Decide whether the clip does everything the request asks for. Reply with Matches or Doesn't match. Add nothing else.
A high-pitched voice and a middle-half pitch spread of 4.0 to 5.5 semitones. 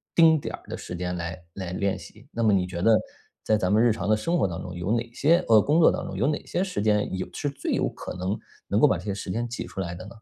Doesn't match